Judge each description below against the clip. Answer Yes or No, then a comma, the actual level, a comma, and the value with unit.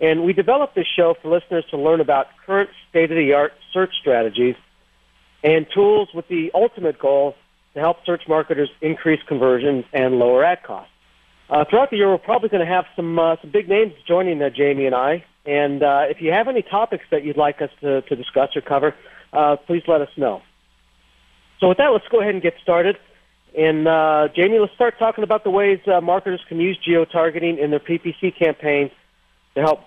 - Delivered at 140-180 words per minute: No, average, 200 wpm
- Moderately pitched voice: Yes, medium, 160 Hz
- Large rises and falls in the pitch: No, average, 4.1 semitones